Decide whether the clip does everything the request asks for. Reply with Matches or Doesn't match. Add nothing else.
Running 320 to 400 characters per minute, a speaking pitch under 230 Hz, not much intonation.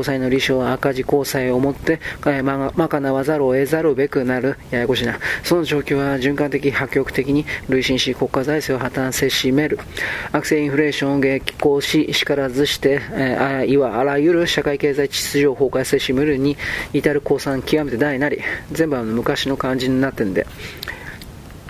Matches